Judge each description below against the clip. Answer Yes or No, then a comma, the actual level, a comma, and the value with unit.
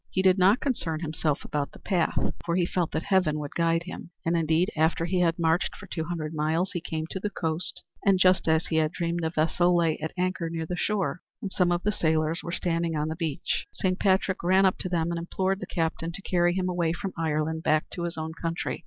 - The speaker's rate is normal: No, fast, 240 wpm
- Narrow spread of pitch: Yes, narrow, 2.3 semitones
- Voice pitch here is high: No, medium, 170 Hz